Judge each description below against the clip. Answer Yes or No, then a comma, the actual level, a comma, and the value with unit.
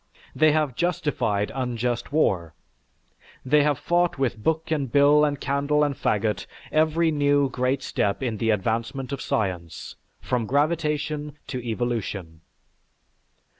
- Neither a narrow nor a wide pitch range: Yes, average, 4.6 semitones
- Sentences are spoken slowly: Yes, slow, 130 wpm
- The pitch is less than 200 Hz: Yes, low, 135 Hz